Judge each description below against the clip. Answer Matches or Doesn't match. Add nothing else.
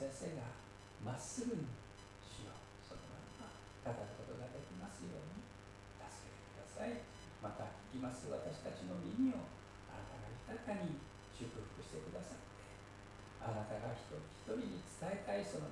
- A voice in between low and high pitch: Doesn't match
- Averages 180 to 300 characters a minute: Matches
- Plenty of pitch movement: Doesn't match